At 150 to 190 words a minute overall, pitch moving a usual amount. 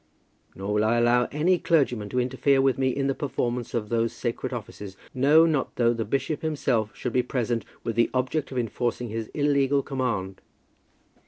Yes: average, 180 wpm; average, 3.0 semitones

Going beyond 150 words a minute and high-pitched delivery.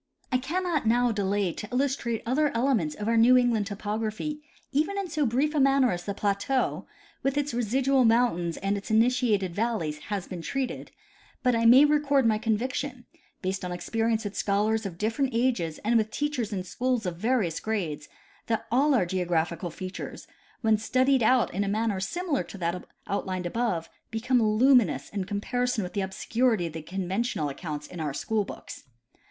Yes: average, 180 wpm; high, 220 Hz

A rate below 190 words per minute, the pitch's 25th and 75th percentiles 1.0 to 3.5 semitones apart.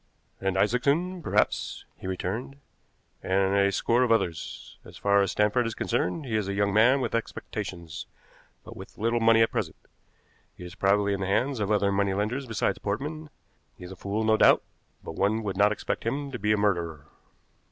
No: average, 195 wpm; average, 3.0 semitones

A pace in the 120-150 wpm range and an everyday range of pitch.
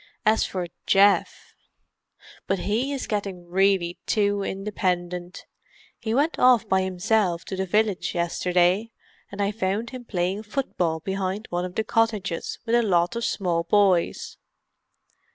Yes: average, 140 wpm; average, 3.3 semitones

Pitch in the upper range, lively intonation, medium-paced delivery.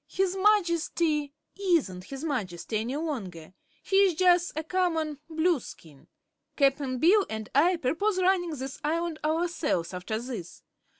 No: very high, 310 Hz; wide, 5.9 semitones; slow, 125 wpm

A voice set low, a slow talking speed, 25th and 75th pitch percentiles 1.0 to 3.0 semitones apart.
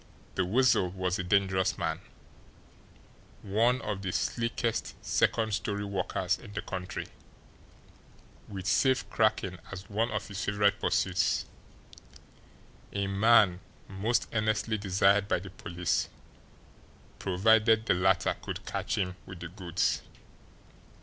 Yes: low, 100 Hz; slow, 120 wpm; average, 2.7 semitones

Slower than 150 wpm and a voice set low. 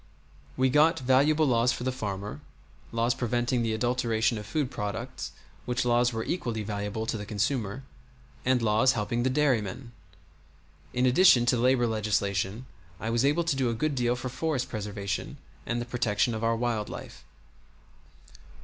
No: average, 160 wpm; low, 120 Hz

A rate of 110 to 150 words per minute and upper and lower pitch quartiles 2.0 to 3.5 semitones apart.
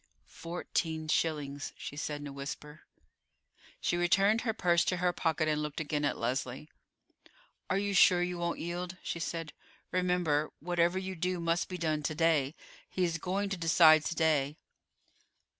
No: average, 165 wpm; average, 2.9 semitones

